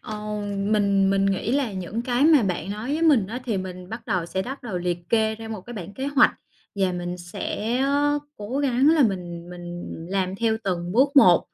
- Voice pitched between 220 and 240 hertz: No, high, 210 Hz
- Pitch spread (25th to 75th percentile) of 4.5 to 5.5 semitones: Yes, average, 5.2 semitones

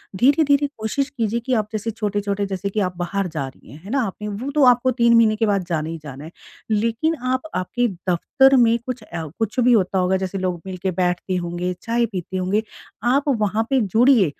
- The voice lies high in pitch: Yes, high, 215 Hz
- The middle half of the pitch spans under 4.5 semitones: No, average, 4.9 semitones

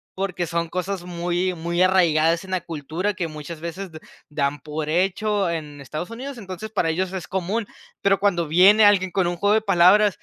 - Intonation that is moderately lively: Yes, average, 3.1 semitones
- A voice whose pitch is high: No, medium, 180 Hz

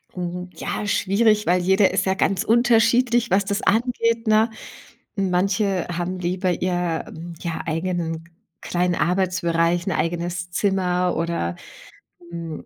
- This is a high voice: No, medium, 180 Hz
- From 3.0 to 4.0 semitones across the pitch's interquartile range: No, narrow, 2.6 semitones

